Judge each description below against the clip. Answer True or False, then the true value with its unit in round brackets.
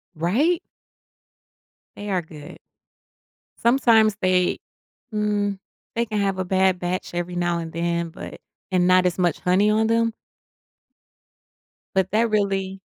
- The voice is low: False (190 Hz)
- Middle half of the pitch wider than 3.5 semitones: False (3.2 semitones)